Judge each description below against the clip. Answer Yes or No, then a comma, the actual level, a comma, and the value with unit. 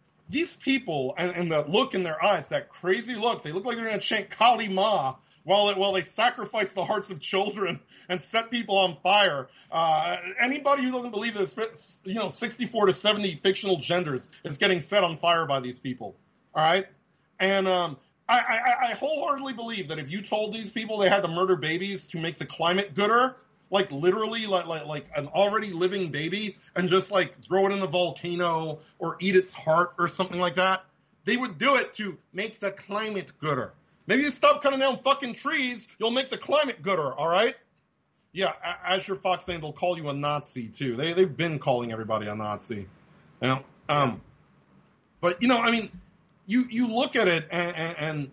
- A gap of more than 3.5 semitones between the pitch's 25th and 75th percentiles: Yes, average, 4.6 semitones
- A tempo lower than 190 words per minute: No, average, 195 wpm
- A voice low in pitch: No, high, 190 Hz